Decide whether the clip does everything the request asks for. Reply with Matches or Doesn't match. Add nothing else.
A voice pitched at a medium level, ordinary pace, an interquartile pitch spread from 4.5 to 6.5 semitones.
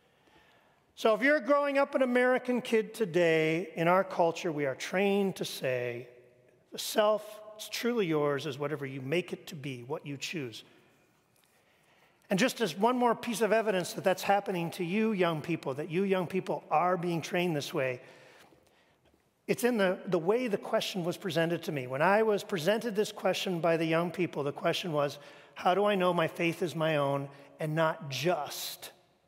Matches